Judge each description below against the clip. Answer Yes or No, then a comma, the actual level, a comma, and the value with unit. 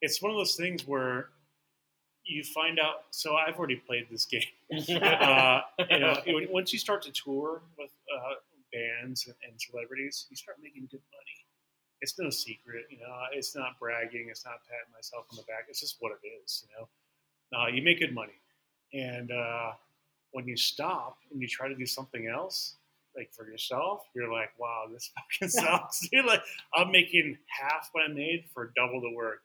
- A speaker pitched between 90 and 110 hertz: No, low, 130 Hz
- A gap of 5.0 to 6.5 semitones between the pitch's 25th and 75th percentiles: Yes, average, 5.3 semitones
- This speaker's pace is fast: No, average, 190 wpm